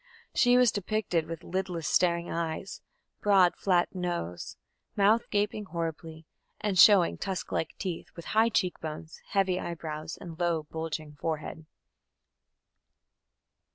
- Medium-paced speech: No, slow, 125 wpm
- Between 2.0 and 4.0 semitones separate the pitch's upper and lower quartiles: Yes, average, 3.4 semitones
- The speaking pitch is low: No, medium, 175 Hz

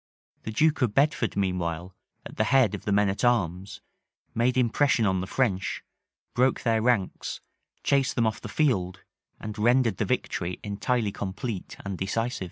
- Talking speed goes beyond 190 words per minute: No, average, 165 wpm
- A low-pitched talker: Yes, low, 110 Hz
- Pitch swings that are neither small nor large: Yes, average, 4.5 semitones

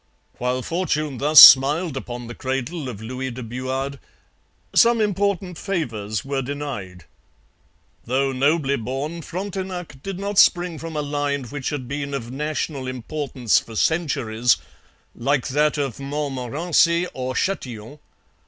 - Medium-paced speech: No, slow, 130 wpm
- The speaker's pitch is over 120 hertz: Yes, medium, 140 Hz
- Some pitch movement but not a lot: Yes, average, 4.1 semitones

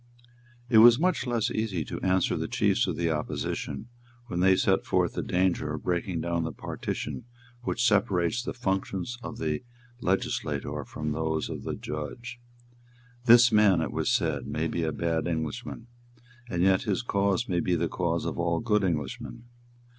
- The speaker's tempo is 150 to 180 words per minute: Yes, average, 170 wpm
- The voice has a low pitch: Yes, very low, 90 Hz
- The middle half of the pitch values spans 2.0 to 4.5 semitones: No, average, 5.1 semitones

